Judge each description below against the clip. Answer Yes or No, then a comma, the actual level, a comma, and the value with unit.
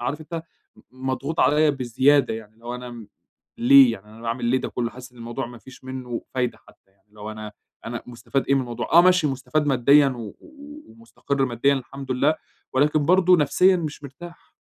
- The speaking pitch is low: Yes, low, 130 Hz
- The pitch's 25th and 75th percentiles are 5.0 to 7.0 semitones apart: No, average, 3.9 semitones